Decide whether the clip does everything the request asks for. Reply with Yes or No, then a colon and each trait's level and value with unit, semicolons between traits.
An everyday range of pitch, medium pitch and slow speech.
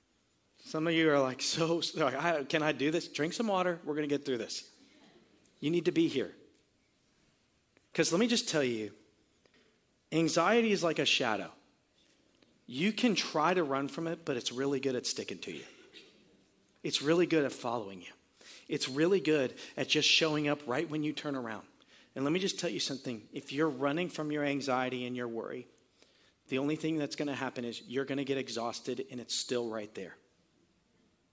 No: average, 3.7 semitones; medium, 150 Hz; average, 200 wpm